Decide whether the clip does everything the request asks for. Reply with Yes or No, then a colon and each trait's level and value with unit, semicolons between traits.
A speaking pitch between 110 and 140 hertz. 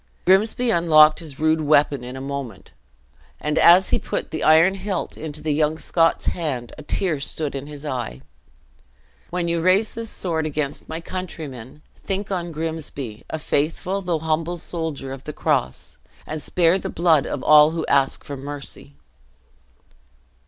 No: medium, 155 Hz